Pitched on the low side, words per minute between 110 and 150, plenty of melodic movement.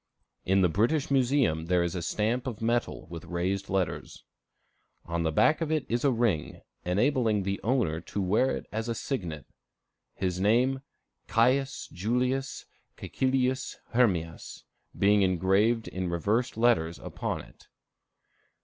Yes: low, 105 Hz; average, 140 wpm; wide, 5.9 semitones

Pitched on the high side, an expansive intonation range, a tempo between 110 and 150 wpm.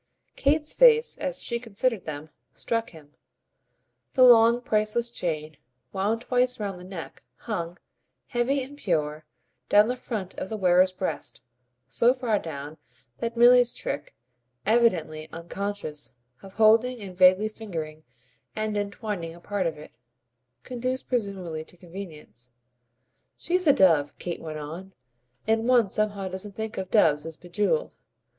Yes: high, 200 Hz; wide, 5.9 semitones; average, 140 wpm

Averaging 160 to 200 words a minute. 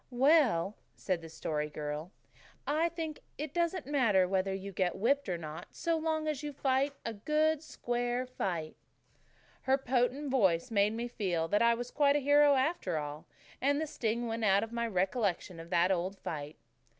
Yes: average, 180 wpm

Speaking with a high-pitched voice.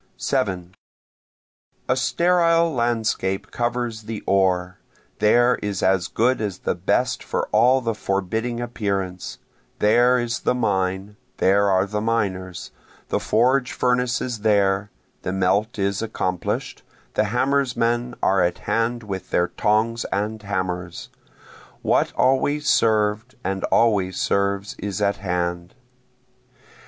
No: low, 105 Hz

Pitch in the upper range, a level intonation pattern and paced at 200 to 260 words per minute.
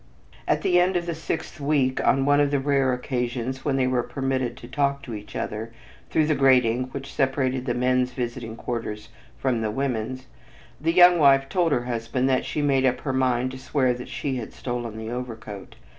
No: low, 130 Hz; narrow, 2.3 semitones; fast, 205 wpm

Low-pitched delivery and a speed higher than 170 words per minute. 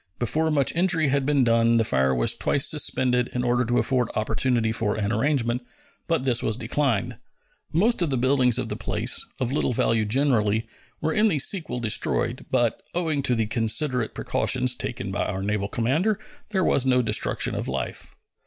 Yes: low, 125 Hz; average, 180 wpm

